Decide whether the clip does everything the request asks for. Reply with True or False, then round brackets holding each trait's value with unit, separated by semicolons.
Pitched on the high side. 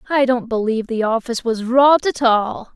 True (240 Hz)